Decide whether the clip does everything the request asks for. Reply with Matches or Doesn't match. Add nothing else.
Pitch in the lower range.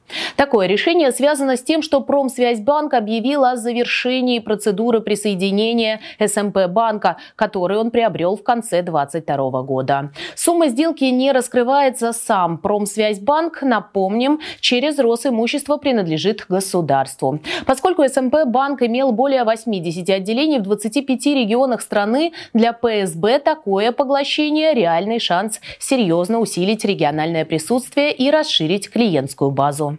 Doesn't match